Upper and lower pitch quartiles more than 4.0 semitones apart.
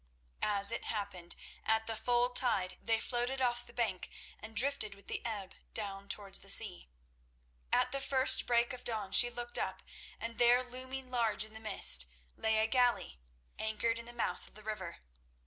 No: average, 2.9 semitones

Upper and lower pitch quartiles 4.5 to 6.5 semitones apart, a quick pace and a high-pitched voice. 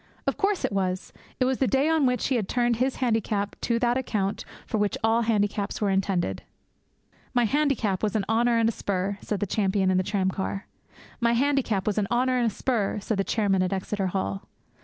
No: average, 3.7 semitones; fast, 210 wpm; high, 215 Hz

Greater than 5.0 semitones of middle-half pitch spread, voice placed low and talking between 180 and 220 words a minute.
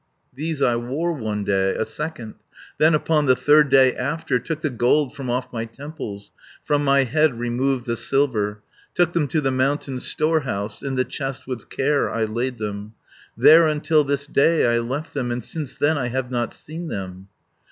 No: average, 4.1 semitones; low, 130 Hz; average, 190 wpm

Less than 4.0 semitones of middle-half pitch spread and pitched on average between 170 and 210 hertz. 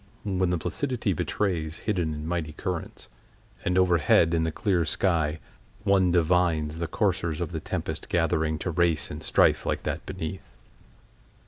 No: narrow, 2.6 semitones; very low, 85 Hz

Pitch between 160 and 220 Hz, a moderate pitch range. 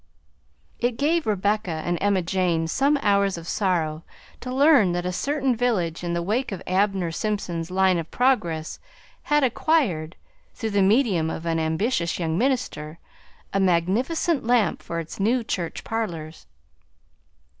No: high, 190 Hz; wide, 6.3 semitones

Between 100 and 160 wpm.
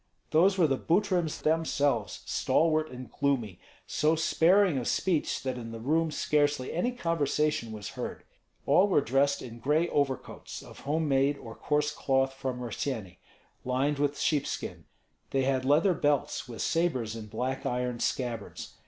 Yes: average, 155 wpm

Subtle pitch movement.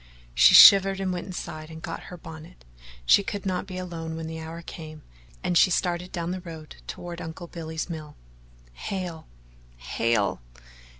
Yes: narrow, 2.2 semitones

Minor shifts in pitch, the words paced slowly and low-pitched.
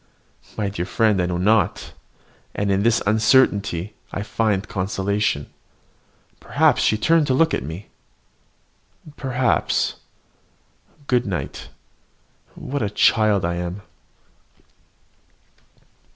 No: average, 3.0 semitones; slow, 105 wpm; low, 105 Hz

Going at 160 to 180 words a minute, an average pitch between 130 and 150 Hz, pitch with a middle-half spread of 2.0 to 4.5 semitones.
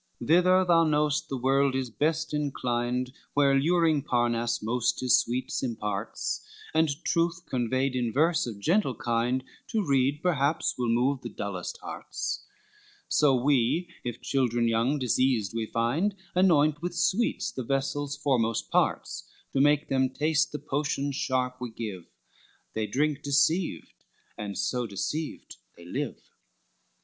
No: average, 140 wpm; low, 135 Hz; average, 4.0 semitones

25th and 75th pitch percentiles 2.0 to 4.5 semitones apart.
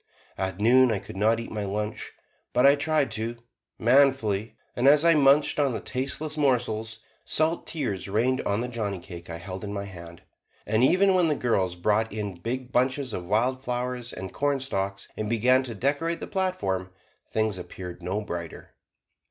No: average, 5.2 semitones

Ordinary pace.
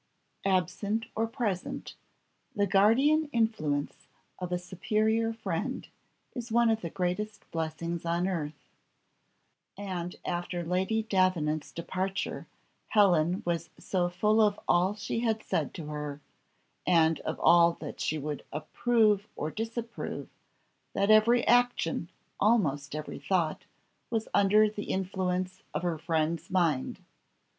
No: slow, 125 wpm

